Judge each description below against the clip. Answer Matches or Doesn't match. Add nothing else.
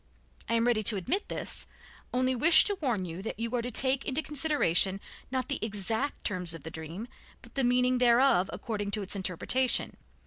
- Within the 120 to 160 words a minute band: Doesn't match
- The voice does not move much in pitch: Doesn't match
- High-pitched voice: Matches